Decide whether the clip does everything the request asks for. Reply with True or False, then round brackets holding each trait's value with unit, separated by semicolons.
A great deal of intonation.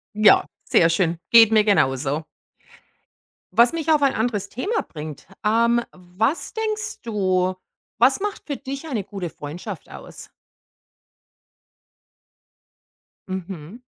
True (6.4 semitones)